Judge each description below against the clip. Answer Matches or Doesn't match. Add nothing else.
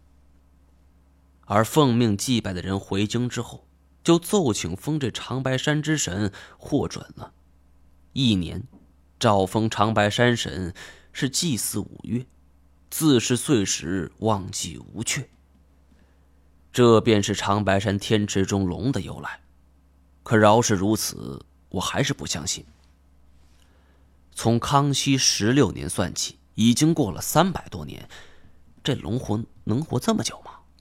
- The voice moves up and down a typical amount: Doesn't match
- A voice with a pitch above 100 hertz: Doesn't match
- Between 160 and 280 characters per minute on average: Matches